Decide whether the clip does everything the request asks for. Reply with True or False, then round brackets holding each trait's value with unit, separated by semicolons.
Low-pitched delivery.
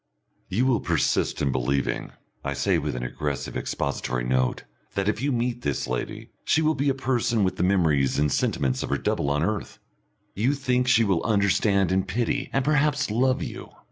True (100 Hz)